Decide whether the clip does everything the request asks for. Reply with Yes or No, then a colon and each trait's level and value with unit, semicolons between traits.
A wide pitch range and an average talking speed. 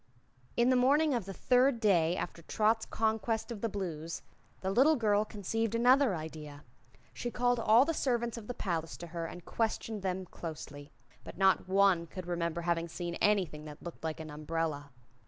Yes: wide, 5.7 semitones; average, 180 wpm